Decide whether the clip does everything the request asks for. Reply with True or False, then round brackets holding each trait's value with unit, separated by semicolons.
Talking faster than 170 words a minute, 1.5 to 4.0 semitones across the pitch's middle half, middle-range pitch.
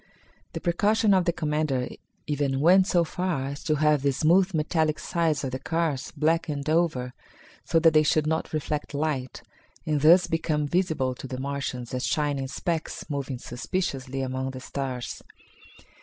False (160 wpm; 3.5 semitones; 150 Hz)